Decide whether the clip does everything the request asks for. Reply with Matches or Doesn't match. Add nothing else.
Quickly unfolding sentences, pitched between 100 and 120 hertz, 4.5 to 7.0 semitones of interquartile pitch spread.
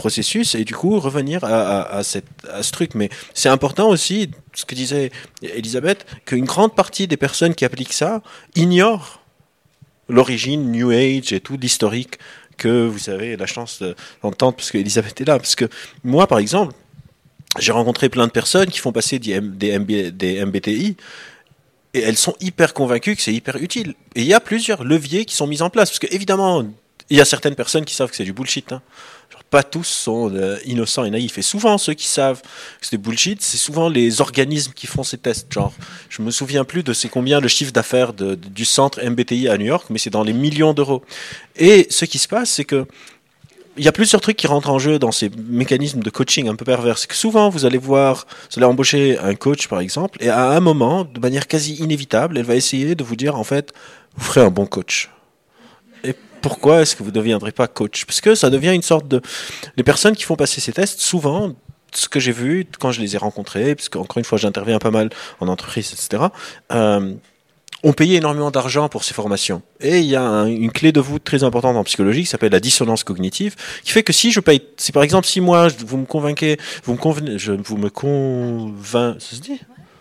Doesn't match